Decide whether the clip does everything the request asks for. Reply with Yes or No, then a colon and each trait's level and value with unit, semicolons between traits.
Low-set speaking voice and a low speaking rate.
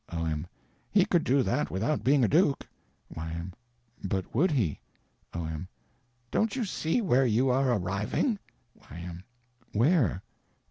Yes: low, 120 Hz; slow, 130 wpm